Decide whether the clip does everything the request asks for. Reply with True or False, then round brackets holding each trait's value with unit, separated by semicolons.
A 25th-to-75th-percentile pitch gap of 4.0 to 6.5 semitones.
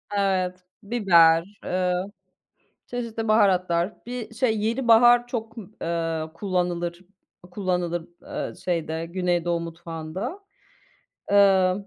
True (4.4 semitones)